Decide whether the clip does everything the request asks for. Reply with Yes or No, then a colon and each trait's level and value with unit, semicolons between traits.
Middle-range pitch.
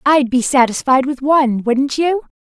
No: very high, 270 Hz